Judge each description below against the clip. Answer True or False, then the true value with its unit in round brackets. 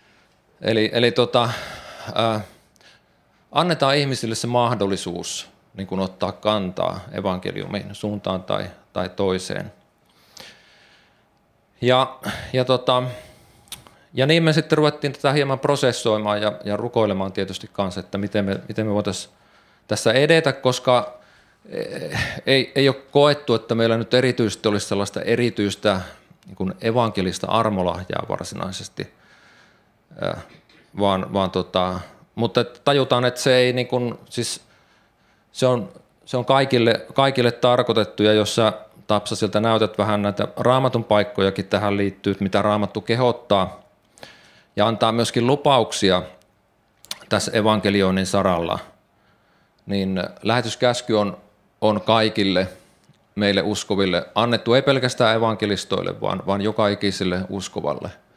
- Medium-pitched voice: False (110 Hz)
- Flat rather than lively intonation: False (3.7 semitones)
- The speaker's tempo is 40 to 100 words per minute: False (115 wpm)